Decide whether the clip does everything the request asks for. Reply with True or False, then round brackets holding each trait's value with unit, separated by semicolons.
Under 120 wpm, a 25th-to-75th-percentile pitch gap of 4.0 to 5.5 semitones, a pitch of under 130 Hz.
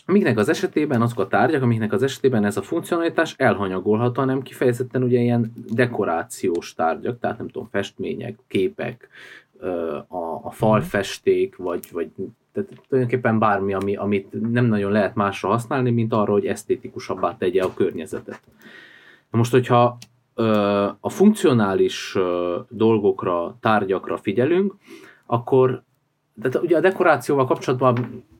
False (125 wpm; 4.3 semitones; 120 Hz)